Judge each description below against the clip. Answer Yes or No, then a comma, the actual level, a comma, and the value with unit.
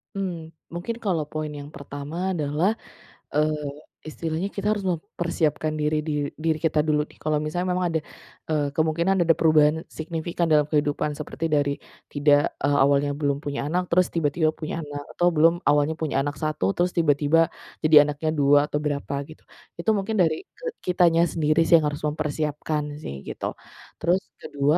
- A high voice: No, medium, 155 Hz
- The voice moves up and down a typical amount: No, narrow, 2.3 semitones